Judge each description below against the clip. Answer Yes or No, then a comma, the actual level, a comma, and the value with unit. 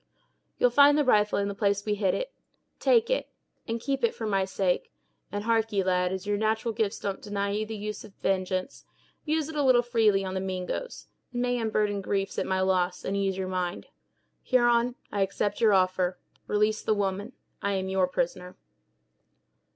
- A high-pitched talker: Yes, high, 205 Hz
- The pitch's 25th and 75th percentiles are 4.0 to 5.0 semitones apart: No, average, 3.3 semitones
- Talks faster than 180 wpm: Yes, average, 190 wpm